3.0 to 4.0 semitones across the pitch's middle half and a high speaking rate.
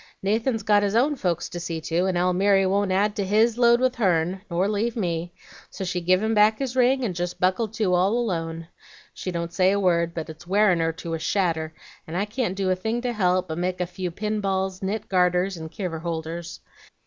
Yes: average, 3.4 semitones; fast, 220 wpm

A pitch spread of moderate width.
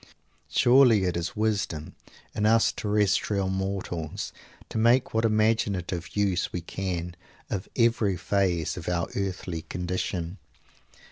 Yes: average, 3.4 semitones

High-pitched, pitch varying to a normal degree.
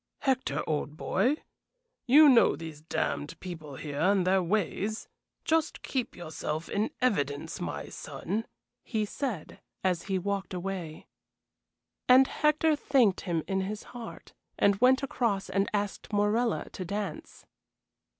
No: high, 200 Hz; wide, 5.7 semitones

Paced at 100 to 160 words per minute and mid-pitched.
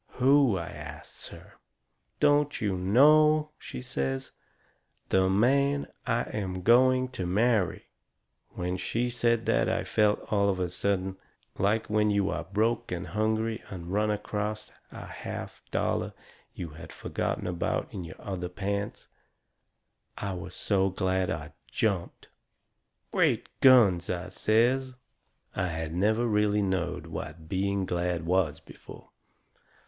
No: slow, 135 wpm; low, 100 Hz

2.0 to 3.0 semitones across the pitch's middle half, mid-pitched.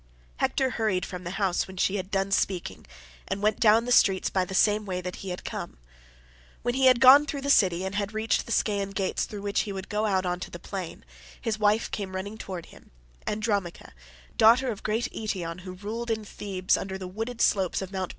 No: average, 2.7 semitones; high, 200 Hz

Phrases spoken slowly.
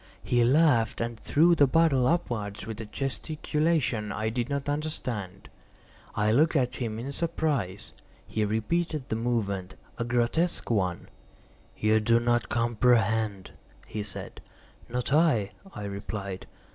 Yes: slow, 130 wpm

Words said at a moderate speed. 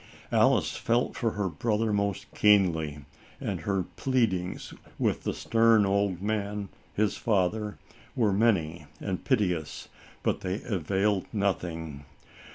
No: slow, 120 wpm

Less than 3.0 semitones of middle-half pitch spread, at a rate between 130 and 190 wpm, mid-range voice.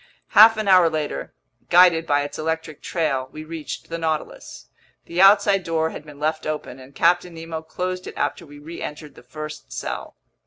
Yes: narrow, 2.5 semitones; average, 180 wpm; medium, 160 Hz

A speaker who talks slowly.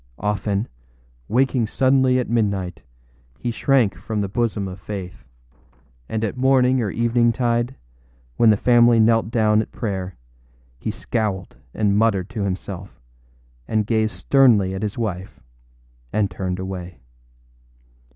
Yes: slow, 130 wpm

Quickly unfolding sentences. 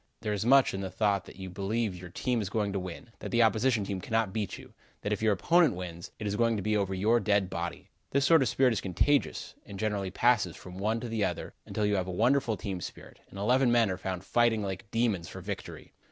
Yes: fast, 250 wpm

